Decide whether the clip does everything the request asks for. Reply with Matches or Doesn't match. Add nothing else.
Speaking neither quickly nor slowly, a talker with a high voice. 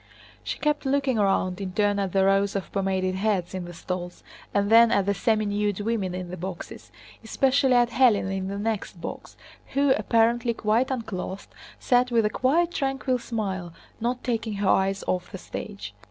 Matches